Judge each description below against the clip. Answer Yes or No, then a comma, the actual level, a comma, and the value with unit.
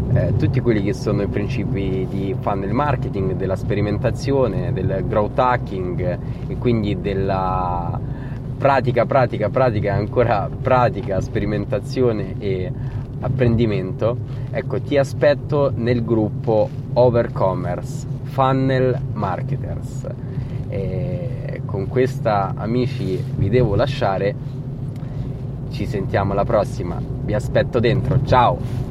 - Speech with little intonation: Yes, narrow, 2.1 semitones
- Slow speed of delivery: Yes, slow, 100 wpm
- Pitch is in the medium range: No, low, 125 Hz